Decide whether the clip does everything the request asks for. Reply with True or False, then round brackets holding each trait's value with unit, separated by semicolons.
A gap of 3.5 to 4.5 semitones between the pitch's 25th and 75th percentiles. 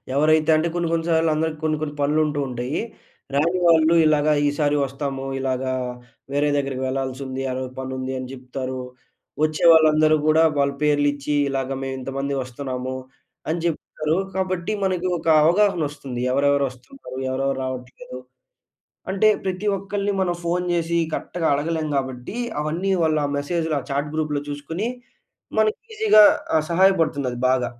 True (3.8 semitones)